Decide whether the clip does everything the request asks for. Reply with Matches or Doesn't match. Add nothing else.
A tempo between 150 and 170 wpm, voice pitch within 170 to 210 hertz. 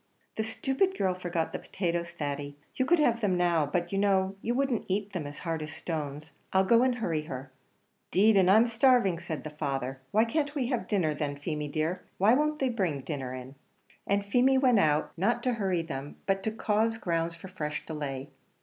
Doesn't match